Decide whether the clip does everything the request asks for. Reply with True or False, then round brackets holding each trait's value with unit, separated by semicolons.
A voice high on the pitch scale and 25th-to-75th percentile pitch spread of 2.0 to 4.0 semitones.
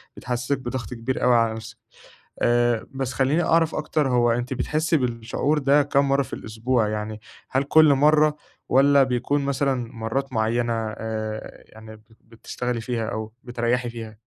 False (125 Hz; 3.4 semitones)